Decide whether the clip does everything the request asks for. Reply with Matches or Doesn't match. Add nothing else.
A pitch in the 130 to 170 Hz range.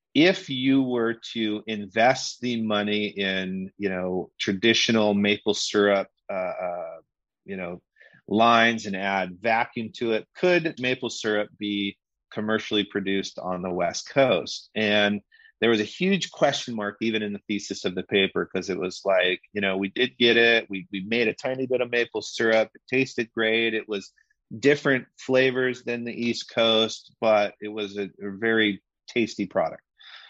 Doesn't match